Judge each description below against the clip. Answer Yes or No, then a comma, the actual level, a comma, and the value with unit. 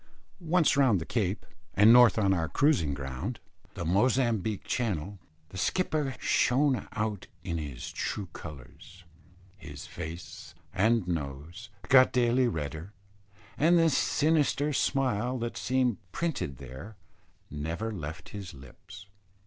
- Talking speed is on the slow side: Yes, slow, 125 wpm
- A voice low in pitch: Yes, low, 105 Hz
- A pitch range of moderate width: No, wide, 7.7 semitones